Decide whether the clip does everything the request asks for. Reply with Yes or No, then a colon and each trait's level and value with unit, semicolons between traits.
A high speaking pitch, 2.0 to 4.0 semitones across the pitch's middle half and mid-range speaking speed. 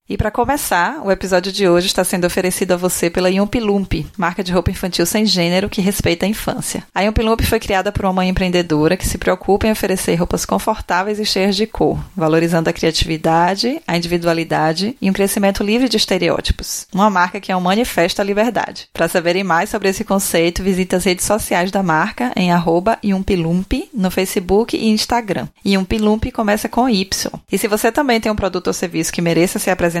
No: high, 195 Hz; average, 3.3 semitones; fast, 195 wpm